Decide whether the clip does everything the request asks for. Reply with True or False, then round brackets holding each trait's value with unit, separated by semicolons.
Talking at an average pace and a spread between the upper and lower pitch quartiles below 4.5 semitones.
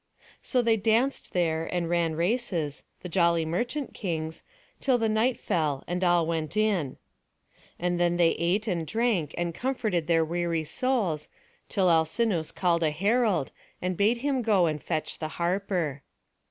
False (155 wpm; 5.0 semitones)